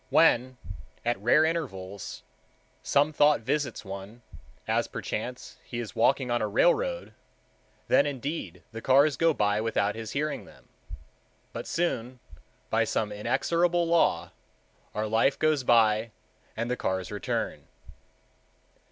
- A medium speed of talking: No, slow, 125 wpm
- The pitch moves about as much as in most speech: No, wide, 5.7 semitones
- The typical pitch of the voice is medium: No, low, 125 Hz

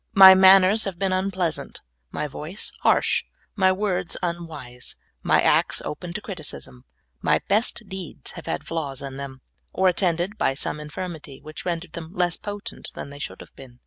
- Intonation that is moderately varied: Yes, average, 4.2 semitones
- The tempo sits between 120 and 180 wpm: Yes, average, 170 wpm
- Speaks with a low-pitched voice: No, medium, 175 Hz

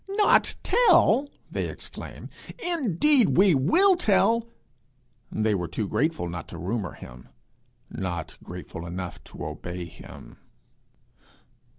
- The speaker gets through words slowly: Yes, slow, 110 wpm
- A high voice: No, medium, 155 Hz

